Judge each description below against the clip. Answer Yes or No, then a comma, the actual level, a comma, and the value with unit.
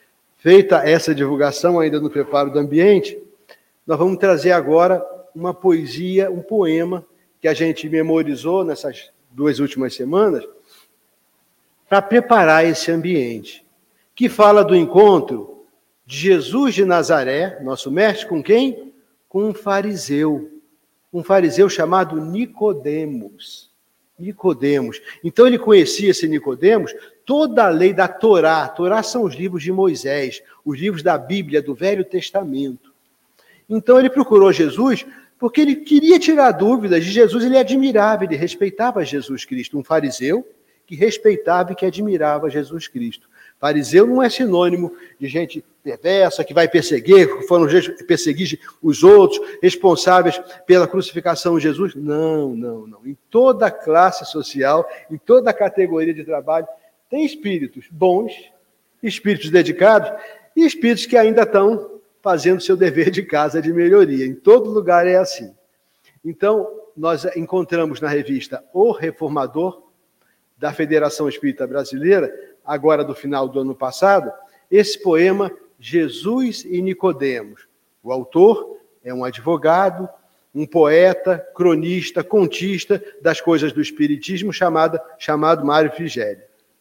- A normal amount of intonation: No, wide, 6.5 semitones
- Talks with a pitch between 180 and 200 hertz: Yes, medium, 185 Hz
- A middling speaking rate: Yes, average, 130 wpm